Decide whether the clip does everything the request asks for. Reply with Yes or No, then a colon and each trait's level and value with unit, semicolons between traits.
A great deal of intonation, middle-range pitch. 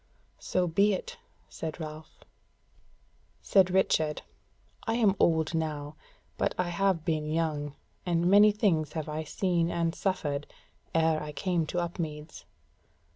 No: average, 3.0 semitones; medium, 165 Hz